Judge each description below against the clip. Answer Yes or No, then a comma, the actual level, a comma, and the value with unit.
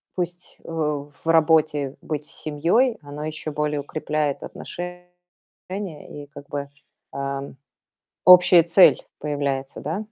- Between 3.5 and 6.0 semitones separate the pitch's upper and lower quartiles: No, average, 3.1 semitones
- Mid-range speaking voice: Yes, medium, 155 Hz